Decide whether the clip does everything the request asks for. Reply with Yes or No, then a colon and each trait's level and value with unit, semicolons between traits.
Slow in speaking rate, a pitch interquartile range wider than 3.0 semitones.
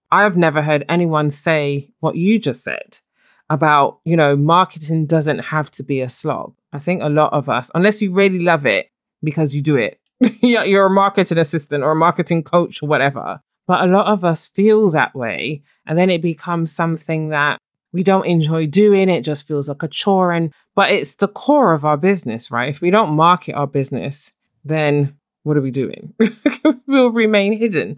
No: average, 195 wpm; average, 4.7 semitones